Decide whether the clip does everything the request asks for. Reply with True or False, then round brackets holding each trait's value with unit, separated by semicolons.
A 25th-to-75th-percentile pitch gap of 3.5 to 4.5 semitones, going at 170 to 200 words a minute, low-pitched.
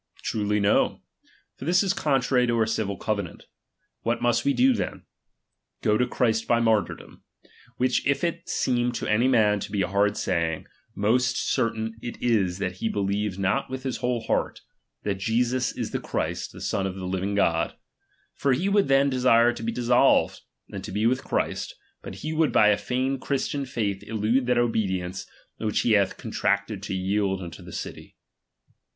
True (4.0 semitones; 180 wpm; 115 Hz)